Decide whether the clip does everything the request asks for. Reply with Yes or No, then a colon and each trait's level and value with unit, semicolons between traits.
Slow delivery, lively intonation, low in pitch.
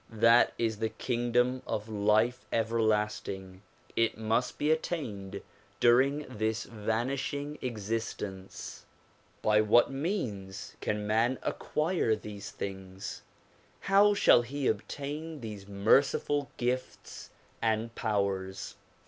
No: slow, 105 wpm; average, 3.8 semitones; low, 115 Hz